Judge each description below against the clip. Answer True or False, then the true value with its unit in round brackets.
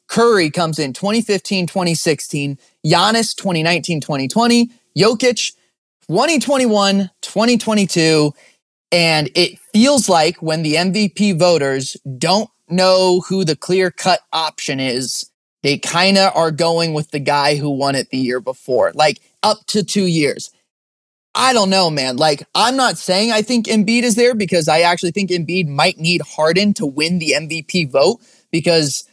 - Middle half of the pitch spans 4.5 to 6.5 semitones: True (5.1 semitones)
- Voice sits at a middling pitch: True (175 Hz)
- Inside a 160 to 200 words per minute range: False (150 wpm)